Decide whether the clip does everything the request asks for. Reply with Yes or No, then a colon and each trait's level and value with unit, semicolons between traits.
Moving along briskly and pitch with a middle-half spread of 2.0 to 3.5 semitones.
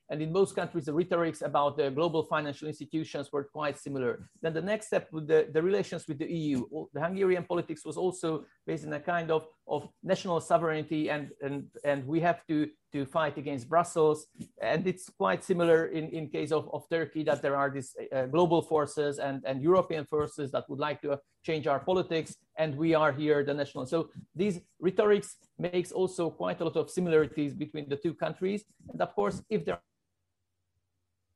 Yes: fast, 195 wpm; average, 2.9 semitones